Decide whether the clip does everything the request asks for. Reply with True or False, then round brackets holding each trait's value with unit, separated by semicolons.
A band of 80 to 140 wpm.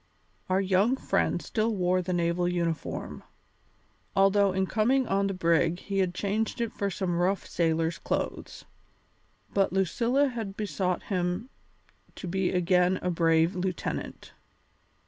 True (135 wpm)